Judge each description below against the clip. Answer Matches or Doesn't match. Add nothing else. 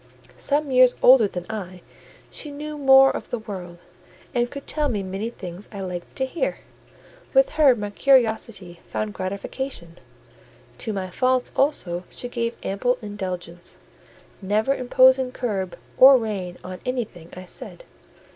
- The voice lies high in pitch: Matches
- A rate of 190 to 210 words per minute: Doesn't match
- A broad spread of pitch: Matches